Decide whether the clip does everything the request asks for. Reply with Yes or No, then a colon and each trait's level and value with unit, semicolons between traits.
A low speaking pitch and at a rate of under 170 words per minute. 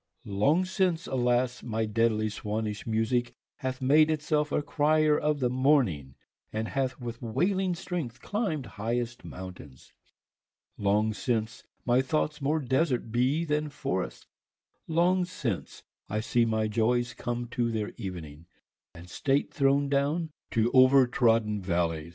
Yes: low, 125 Hz; average, 150 wpm